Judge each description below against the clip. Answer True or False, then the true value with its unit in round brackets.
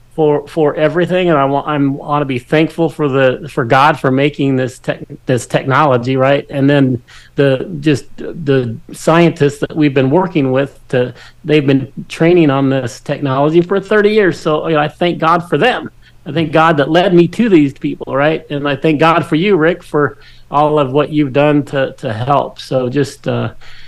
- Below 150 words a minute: False (200 wpm)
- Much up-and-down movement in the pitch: False (2.8 semitones)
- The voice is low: False (145 Hz)